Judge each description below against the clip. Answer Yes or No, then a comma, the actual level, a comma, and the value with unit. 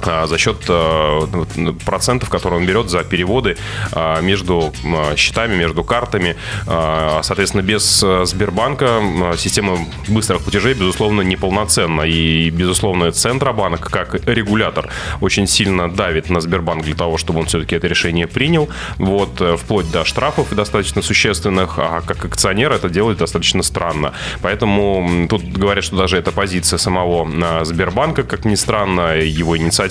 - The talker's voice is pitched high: No, very low, 90 Hz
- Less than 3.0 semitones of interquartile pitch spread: No, average, 3.3 semitones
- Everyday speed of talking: Yes, average, 130 wpm